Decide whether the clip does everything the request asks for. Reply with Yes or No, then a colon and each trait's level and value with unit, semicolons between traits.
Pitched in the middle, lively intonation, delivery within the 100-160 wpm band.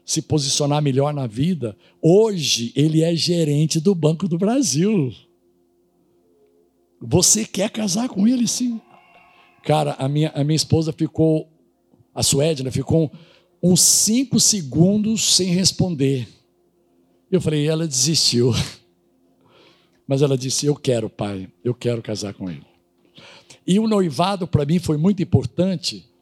Yes: medium, 150 Hz; wide, 6.7 semitones; average, 135 wpm